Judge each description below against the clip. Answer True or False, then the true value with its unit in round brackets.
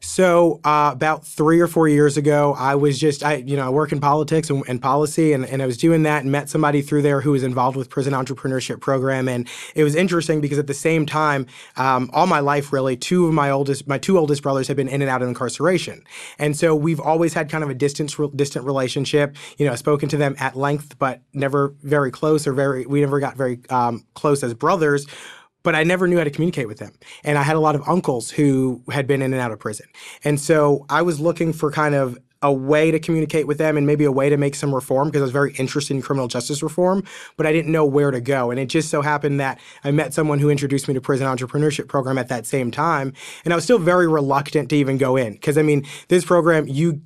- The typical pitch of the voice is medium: True (145 Hz)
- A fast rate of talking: True (255 wpm)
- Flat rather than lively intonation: True (2.2 semitones)